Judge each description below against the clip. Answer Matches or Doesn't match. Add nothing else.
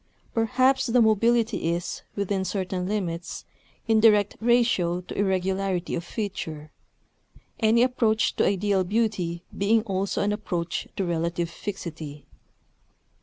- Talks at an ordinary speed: Doesn't match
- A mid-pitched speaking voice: Doesn't match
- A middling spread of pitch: Matches